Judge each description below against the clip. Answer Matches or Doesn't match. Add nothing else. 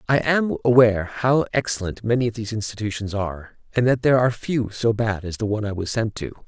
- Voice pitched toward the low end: Matches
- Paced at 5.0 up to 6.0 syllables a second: Doesn't match